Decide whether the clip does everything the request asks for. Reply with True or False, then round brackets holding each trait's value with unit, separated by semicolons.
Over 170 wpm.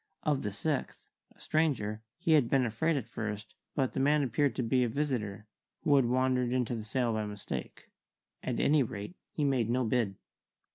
True (190 wpm)